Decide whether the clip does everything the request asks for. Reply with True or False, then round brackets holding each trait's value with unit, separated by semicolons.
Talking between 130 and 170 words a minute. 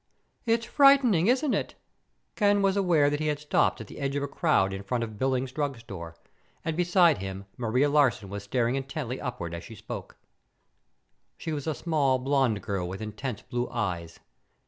False (180 wpm)